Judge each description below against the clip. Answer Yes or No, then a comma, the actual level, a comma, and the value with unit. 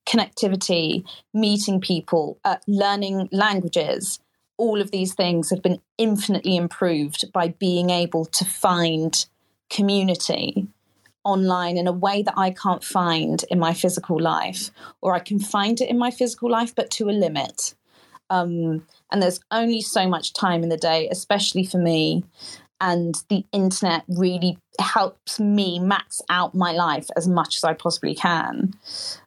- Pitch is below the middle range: No, medium, 185 Hz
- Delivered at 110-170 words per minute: Yes, average, 150 wpm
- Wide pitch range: No, average, 2.9 semitones